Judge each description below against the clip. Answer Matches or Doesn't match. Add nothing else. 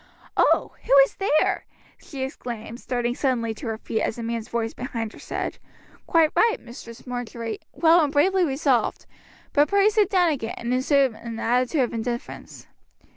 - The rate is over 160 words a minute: Matches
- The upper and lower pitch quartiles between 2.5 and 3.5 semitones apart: Doesn't match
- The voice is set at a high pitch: Matches